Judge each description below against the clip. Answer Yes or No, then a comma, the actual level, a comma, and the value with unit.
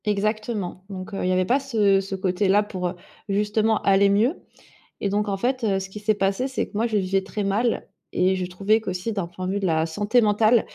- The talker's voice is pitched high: Yes, high, 200 Hz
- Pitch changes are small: Yes, narrow, 2.3 semitones